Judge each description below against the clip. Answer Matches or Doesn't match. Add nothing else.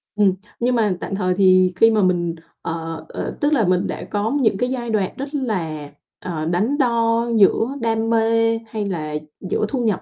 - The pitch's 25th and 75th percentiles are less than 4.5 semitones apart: Matches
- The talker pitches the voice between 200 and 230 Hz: Matches